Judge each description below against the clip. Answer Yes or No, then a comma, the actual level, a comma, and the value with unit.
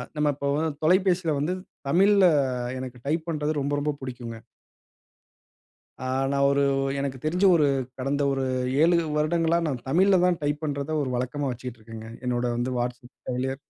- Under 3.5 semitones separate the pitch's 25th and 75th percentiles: No, average, 4.0 semitones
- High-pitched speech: No, medium, 140 Hz